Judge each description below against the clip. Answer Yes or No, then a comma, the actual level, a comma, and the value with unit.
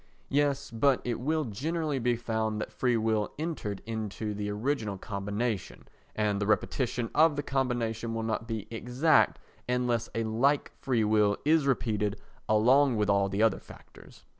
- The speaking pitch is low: Yes, low, 115 Hz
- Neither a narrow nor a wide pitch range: Yes, average, 3.9 semitones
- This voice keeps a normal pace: Yes, average, 160 wpm